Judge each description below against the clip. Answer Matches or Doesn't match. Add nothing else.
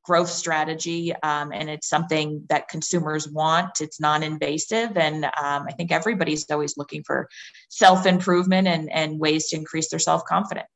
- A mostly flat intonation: Matches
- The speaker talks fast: Doesn't match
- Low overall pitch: Doesn't match